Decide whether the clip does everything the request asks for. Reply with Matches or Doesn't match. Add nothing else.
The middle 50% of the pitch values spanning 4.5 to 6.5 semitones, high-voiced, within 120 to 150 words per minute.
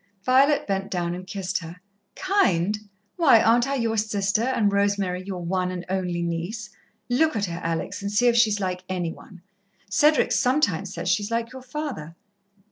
Doesn't match